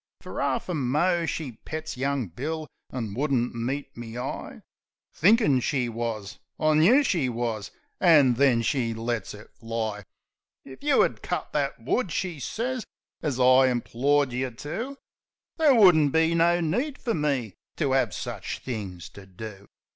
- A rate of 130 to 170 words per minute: Yes, average, 155 wpm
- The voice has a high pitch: No, low, 135 Hz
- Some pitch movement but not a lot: No, wide, 5.7 semitones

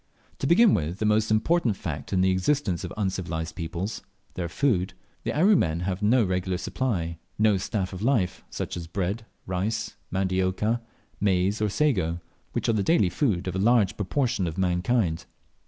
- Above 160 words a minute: Yes, average, 170 wpm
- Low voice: Yes, very low, 95 Hz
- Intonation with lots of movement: No, average, 3.6 semitones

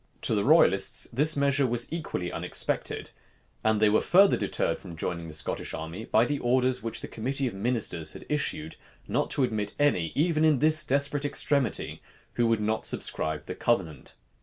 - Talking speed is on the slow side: No, average, 180 wpm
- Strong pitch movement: Yes, wide, 6.3 semitones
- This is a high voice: No, low, 120 Hz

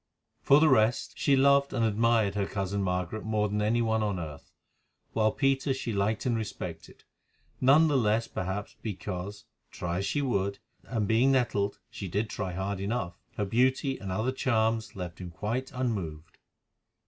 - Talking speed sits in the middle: Yes, average, 160 wpm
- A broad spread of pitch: No, average, 4.0 semitones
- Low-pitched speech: Yes, low, 110 Hz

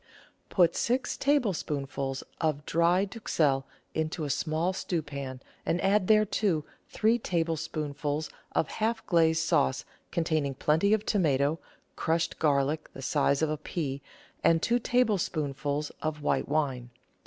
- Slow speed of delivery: Yes, slow, 130 wpm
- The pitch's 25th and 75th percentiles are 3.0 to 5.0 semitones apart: Yes, average, 4.3 semitones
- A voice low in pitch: No, medium, 160 Hz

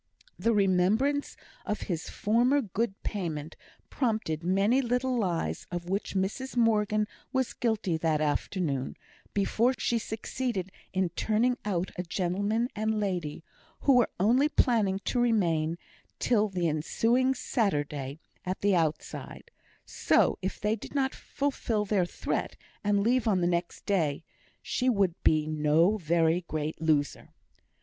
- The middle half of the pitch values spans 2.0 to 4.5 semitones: No, average, 5.2 semitones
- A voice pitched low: No, high, 200 Hz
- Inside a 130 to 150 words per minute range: Yes, slow, 135 wpm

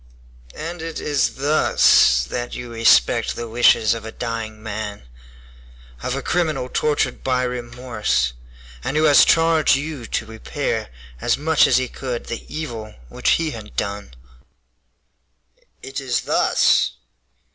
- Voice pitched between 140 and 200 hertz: No, low, 125 Hz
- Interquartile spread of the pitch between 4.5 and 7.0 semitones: Yes, average, 4.8 semitones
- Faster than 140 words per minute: No, slow, 135 wpm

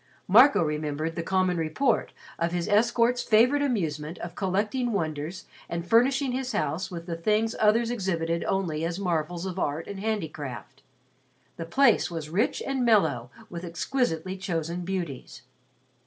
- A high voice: No, medium, 180 Hz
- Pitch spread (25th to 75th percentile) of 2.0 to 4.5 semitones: No, average, 5.3 semitones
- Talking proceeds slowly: No, average, 145 wpm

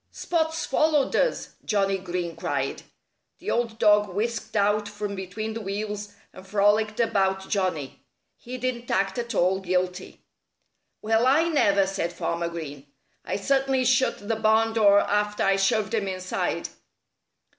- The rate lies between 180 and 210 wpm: No, average, 145 wpm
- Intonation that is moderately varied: Yes, average, 3.0 semitones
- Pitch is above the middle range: Yes, high, 205 Hz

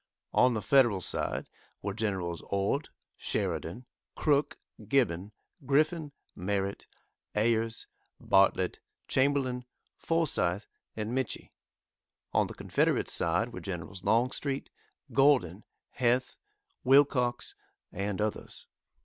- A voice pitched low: Yes, low, 115 Hz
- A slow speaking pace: Yes, slow, 95 wpm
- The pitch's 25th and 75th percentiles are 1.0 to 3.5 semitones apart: No, wide, 5.5 semitones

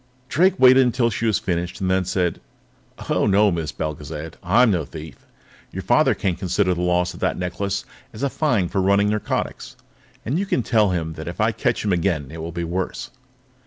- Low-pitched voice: Yes, very low, 95 Hz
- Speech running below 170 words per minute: No, average, 200 wpm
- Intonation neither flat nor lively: Yes, average, 4.0 semitones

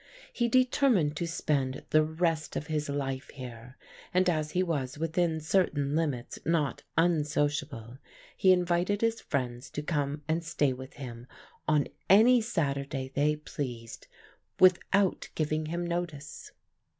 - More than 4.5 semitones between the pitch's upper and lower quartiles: No, average, 3.8 semitones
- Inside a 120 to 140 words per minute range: Yes, slow, 135 wpm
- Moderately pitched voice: Yes, medium, 155 Hz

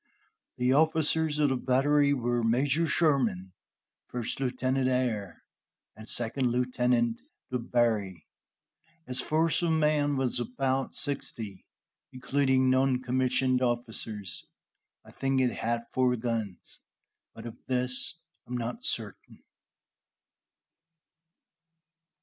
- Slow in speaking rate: Yes, slow, 105 wpm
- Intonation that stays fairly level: Yes, narrow, 2.3 semitones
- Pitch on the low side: Yes, low, 125 Hz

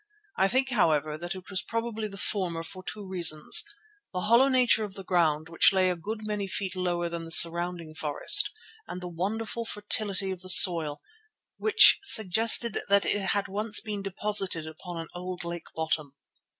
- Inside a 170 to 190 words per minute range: Yes, average, 175 wpm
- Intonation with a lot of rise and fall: No, average, 3.7 semitones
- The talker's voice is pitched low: No, medium, 185 Hz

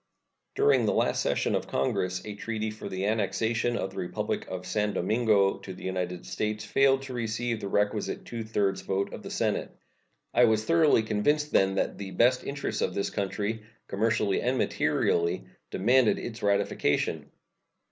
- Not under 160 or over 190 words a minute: Yes, average, 165 wpm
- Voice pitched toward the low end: Yes, low, 110 Hz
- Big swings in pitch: No, average, 3.3 semitones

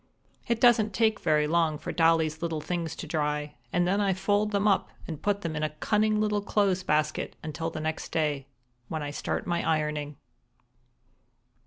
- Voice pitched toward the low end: No, medium, 165 Hz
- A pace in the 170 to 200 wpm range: Yes, average, 180 wpm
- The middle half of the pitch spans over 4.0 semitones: Yes, average, 4.8 semitones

